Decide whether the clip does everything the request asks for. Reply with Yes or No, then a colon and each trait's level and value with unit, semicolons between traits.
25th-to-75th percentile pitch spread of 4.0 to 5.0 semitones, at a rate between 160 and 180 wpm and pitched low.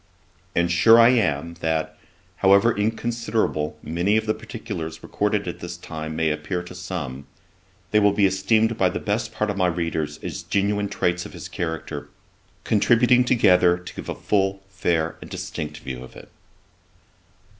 Yes: average, 4.5 semitones; average, 165 wpm; very low, 90 Hz